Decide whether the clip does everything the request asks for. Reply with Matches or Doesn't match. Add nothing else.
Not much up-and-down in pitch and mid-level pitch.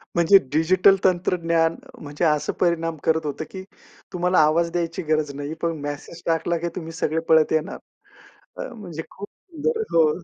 Matches